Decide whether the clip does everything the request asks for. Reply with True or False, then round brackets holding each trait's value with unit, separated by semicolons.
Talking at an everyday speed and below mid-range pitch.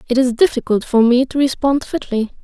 False (195 wpm; 250 Hz)